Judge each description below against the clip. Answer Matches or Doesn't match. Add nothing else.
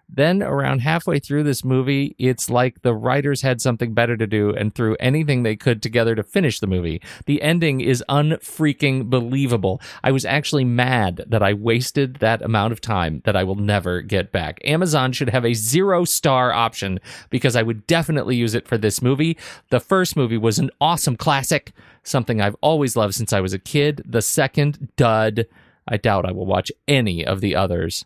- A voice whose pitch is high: Doesn't match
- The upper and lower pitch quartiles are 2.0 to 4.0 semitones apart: Doesn't match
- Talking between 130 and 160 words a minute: Doesn't match